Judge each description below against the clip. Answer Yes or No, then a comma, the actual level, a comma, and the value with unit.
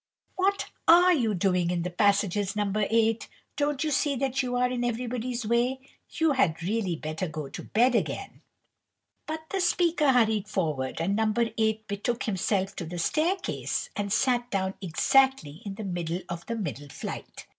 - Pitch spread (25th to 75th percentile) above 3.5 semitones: Yes, wide, 5.6 semitones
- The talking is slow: No, average, 170 wpm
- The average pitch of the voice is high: Yes, high, 220 Hz